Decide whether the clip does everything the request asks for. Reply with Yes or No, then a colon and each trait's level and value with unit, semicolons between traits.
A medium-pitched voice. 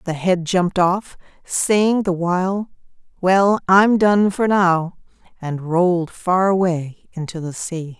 Yes: medium, 180 Hz